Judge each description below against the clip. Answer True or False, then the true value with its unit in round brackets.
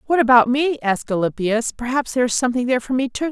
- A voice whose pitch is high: True (250 Hz)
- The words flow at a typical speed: False (235 wpm)